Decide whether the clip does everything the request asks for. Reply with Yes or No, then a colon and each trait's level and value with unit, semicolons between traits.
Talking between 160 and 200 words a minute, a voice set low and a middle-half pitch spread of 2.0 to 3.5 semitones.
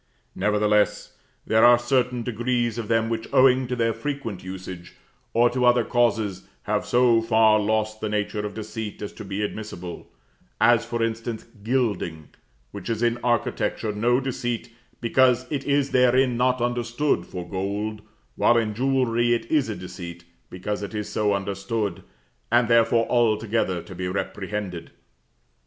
No: average, 150 wpm; low, 115 Hz; narrow, 2.6 semitones